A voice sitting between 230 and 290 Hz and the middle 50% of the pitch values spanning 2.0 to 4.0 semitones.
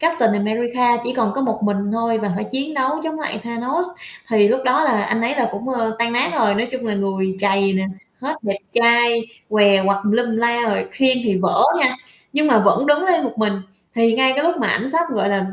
Yes: high, 235 Hz; average, 3.7 semitones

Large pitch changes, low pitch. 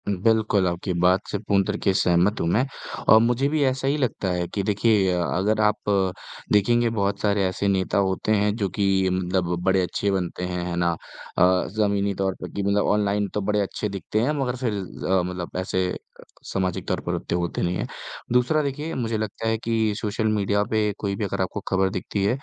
No: average, 2.7 semitones; low, 100 Hz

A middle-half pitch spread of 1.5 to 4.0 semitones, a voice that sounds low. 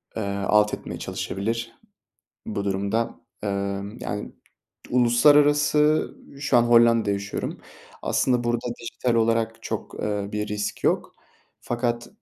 Yes: narrow, 2.6 semitones; low, 115 Hz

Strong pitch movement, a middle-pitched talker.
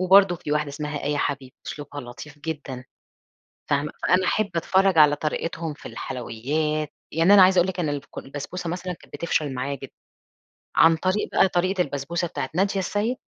No: average, 4.2 semitones; medium, 160 Hz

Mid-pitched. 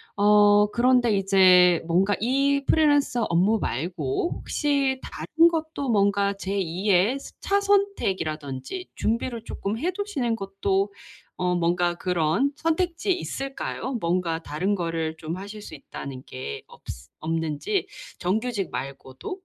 No: high, 200 Hz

